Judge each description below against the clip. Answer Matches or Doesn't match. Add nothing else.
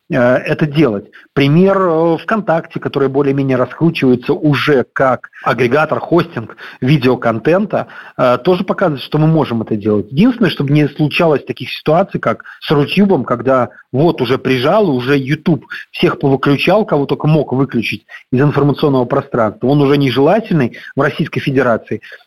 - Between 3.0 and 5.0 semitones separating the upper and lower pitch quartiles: Matches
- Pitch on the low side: Doesn't match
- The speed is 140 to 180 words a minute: Doesn't match